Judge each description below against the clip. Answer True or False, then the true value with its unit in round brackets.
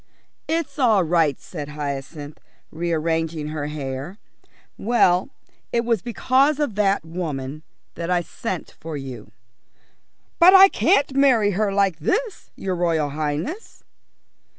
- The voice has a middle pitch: True (175 Hz)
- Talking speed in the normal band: False (125 wpm)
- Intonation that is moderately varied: False (7.5 semitones)